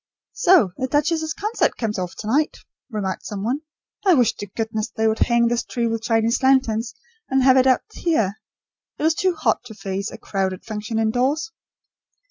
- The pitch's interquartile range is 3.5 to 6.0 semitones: Yes, average, 3.9 semitones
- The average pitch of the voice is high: Yes, high, 235 Hz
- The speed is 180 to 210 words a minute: Yes, average, 185 wpm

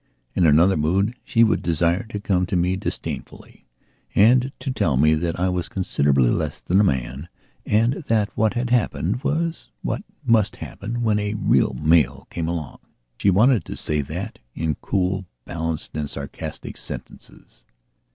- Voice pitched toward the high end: No, very low, 90 Hz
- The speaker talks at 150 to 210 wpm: Yes, average, 160 wpm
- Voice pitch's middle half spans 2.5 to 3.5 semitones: No, average, 5.3 semitones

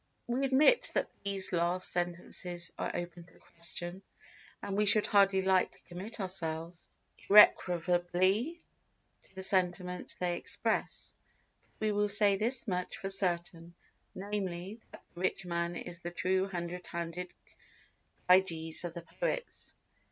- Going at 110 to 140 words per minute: Yes, slow, 135 wpm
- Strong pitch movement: No, narrow, 2.4 semitones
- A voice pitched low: No, medium, 180 Hz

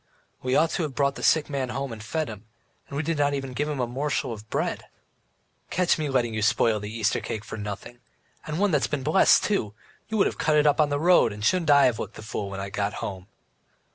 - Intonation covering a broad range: Yes, wide, 5.7 semitones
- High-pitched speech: No, low, 135 Hz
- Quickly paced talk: Yes, fast, 255 wpm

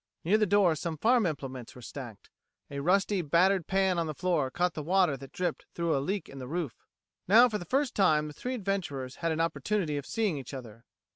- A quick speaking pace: Yes, fast, 225 wpm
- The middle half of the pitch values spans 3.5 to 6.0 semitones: Yes, wide, 5.5 semitones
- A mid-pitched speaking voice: Yes, medium, 170 Hz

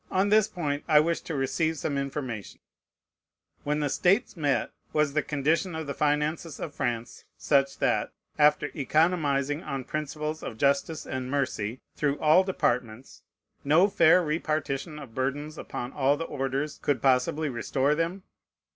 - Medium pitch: Yes, medium, 150 Hz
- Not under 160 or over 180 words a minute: No, average, 150 wpm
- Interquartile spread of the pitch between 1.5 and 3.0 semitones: Yes, narrow, 2.5 semitones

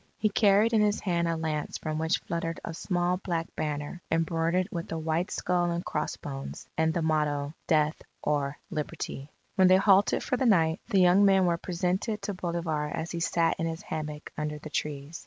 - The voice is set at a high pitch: No, medium, 165 Hz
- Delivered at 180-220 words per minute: Yes, average, 195 wpm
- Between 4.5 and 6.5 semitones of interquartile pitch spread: No, average, 2.9 semitones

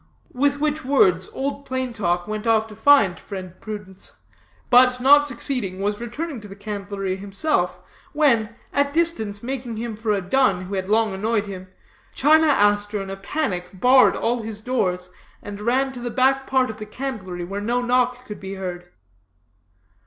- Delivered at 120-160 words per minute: No, average, 175 wpm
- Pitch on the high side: Yes, high, 220 Hz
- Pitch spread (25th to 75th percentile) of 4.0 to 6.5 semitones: Yes, average, 4.8 semitones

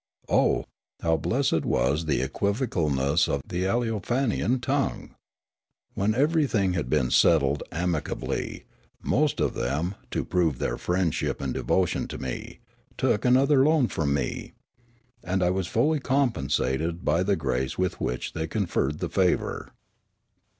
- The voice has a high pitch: No, very low, 90 Hz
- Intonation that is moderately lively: No, wide, 7.5 semitones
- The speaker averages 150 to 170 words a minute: No, slow, 135 wpm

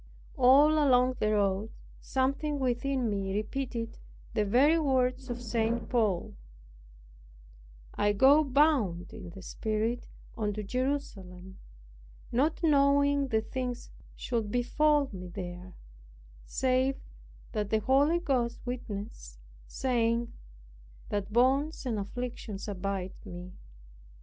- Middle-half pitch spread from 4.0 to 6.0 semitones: Yes, average, 4.6 semitones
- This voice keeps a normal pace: No, slow, 105 wpm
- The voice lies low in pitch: No, high, 240 Hz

